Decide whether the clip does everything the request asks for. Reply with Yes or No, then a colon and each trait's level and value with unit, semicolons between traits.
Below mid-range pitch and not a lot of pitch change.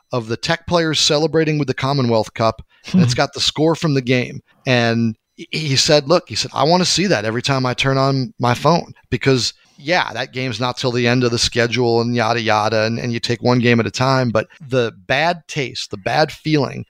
No: low, 130 Hz; average, 3.9 semitones